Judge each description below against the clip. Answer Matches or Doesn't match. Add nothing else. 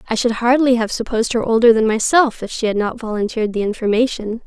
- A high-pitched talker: Matches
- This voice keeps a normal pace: Doesn't match